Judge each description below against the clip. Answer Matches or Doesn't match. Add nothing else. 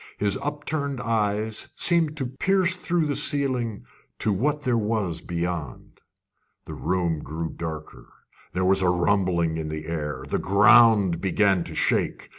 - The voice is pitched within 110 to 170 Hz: Doesn't match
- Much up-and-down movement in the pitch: Matches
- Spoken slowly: Doesn't match